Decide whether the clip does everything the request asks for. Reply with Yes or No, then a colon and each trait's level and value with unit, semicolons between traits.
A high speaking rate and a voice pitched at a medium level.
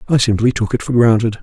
No: fast, 250 wpm; low, 115 Hz